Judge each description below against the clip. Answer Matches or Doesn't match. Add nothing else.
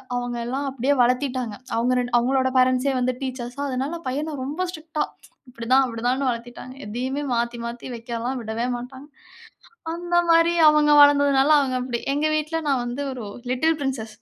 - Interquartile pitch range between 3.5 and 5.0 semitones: Doesn't match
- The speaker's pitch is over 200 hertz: Matches